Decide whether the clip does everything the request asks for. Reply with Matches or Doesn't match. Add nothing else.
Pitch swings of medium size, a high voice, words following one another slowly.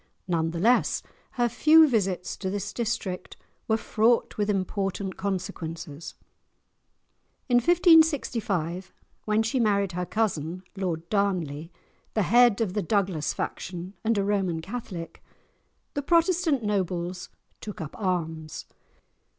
Matches